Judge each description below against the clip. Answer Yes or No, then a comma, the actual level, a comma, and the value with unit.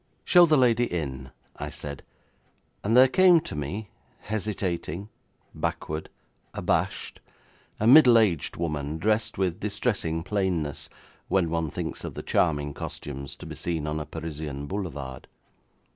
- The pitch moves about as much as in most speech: No, wide, 6.4 semitones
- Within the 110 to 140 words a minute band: Yes, slow, 135 wpm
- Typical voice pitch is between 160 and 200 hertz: No, very low, 85 Hz